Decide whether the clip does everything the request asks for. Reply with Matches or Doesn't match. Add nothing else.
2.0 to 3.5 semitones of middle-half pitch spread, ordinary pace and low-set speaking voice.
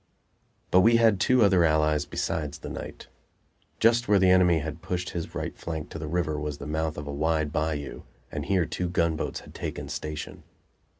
Matches